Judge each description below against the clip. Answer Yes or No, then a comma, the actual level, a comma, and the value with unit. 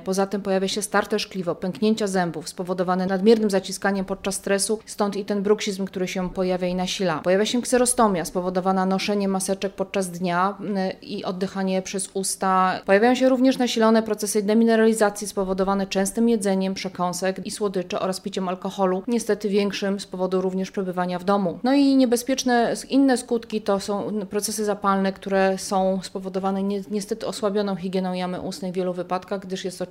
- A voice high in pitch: Yes, high, 195 Hz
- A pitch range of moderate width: No, narrow, 1.9 semitones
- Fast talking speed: Yes, fast, 165 wpm